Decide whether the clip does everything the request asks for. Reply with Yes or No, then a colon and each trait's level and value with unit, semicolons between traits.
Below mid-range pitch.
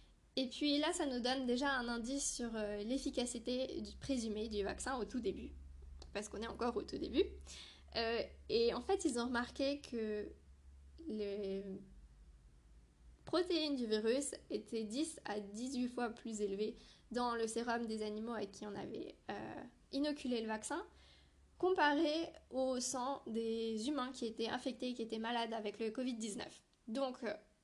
No: high, 235 Hz